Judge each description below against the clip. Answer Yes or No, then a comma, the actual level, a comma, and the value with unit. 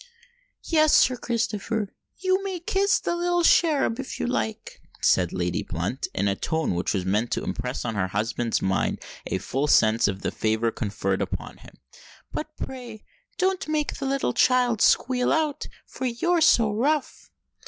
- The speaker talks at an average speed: Yes, average, 160 wpm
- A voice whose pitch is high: Yes, high, 225 Hz